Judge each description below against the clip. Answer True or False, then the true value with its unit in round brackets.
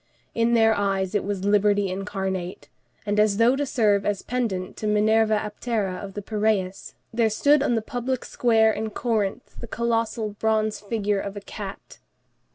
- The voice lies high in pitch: True (210 Hz)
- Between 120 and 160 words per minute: False (170 wpm)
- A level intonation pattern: True (2.2 semitones)